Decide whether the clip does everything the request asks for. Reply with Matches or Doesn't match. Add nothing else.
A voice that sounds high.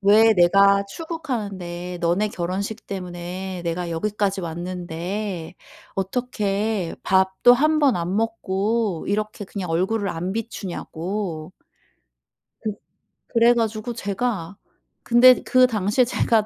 Matches